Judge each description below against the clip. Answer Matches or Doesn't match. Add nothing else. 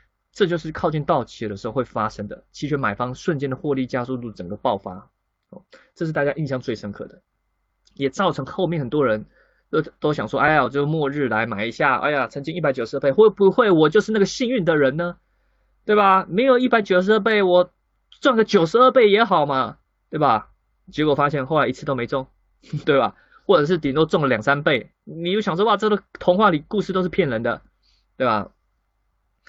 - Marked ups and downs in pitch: Matches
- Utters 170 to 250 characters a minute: Doesn't match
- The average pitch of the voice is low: Doesn't match